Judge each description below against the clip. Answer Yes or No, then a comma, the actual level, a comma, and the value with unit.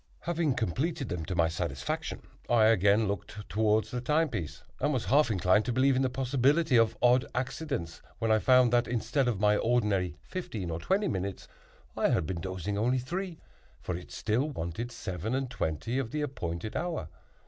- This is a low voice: Yes, low, 115 Hz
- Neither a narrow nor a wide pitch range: No, wide, 6.0 semitones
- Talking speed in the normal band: Yes, average, 185 wpm